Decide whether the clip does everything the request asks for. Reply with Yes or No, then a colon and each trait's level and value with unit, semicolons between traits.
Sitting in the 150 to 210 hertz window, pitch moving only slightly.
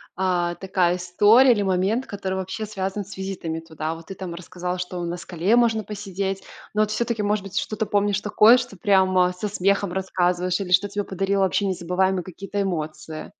Yes: high, 190 Hz; narrow, 2.3 semitones